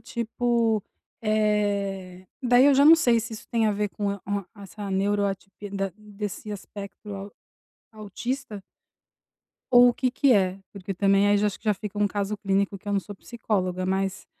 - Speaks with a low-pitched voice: No, high, 205 Hz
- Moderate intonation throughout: No, narrow, 2.0 semitones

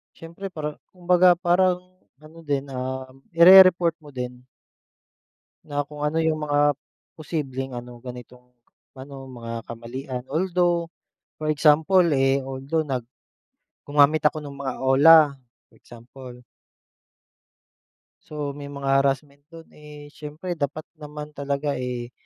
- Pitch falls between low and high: Yes, medium, 145 Hz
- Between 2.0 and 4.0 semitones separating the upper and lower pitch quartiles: Yes, average, 3.3 semitones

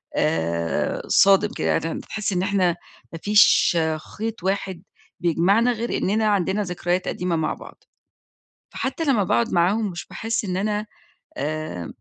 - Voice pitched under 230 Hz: Yes, high, 190 Hz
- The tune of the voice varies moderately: Yes, average, 3.8 semitones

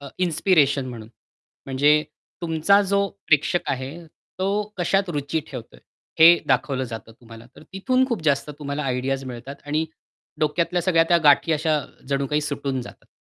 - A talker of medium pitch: Yes, medium, 150 Hz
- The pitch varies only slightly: No, average, 4.1 semitones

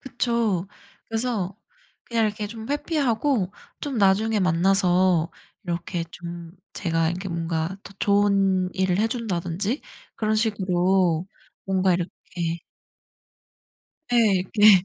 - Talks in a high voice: Yes, high, 195 Hz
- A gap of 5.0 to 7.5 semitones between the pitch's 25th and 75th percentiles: No, average, 3.8 semitones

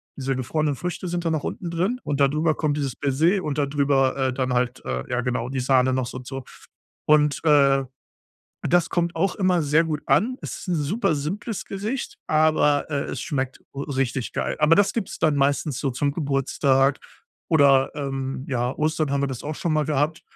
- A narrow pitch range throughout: No, average, 3.2 semitones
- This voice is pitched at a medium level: Yes, medium, 145 Hz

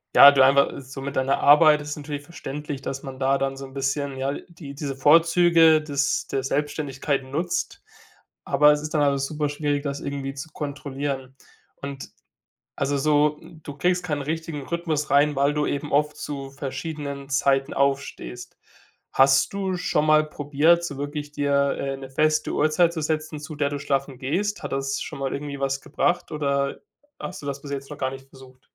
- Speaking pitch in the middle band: Yes, medium, 145 Hz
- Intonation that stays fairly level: Yes, narrow, 1.9 semitones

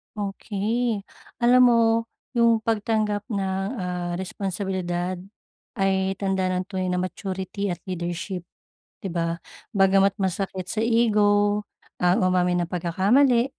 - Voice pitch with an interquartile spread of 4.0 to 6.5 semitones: No, narrow, 2.4 semitones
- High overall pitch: Yes, high, 195 Hz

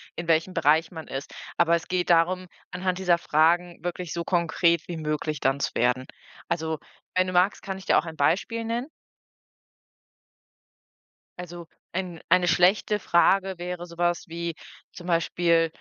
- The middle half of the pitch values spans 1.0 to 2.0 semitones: Yes, narrow, 1.7 semitones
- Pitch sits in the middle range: Yes, medium, 170 Hz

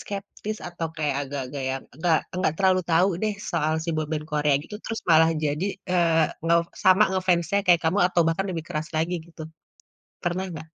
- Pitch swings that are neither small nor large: Yes, average, 3.0 semitones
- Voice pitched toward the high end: No, medium, 165 Hz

